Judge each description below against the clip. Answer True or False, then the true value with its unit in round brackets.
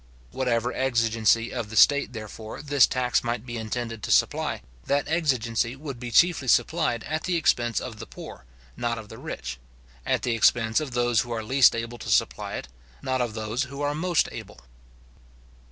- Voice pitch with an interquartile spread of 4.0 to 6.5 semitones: False (3.3 semitones)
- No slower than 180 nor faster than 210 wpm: True (185 wpm)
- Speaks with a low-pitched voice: True (120 Hz)